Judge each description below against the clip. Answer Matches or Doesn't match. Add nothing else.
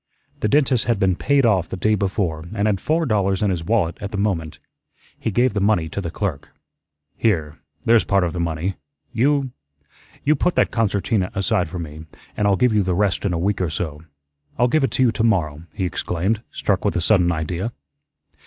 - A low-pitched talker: Matches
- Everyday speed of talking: Doesn't match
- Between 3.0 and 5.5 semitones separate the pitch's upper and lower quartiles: Matches